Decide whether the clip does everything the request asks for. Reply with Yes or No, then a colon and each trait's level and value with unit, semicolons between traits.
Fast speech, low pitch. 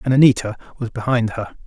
No: average, 180 wpm; low, 120 Hz